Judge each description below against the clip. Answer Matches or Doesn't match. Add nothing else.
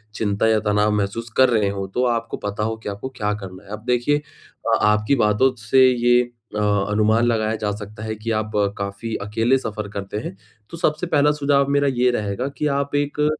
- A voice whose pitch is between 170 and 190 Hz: Doesn't match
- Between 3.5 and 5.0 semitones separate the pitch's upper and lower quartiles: Matches